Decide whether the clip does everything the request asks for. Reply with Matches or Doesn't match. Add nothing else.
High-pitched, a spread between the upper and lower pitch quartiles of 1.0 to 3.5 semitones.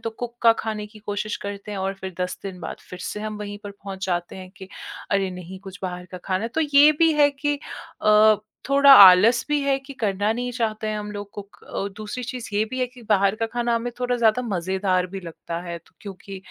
Doesn't match